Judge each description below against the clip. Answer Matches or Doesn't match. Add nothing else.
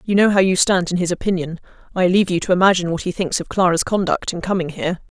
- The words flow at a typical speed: Doesn't match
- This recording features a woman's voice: Matches